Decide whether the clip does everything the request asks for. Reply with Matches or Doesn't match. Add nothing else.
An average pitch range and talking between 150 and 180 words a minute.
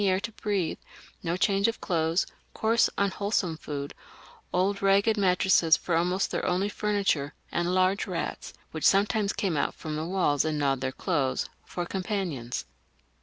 Matches